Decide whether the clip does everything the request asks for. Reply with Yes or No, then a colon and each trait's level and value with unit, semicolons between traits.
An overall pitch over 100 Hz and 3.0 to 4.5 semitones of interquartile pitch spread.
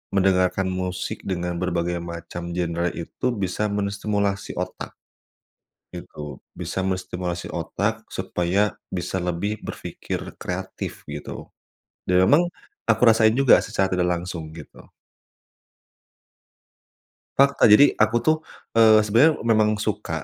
No: very low, 95 Hz; average, 3.3 semitones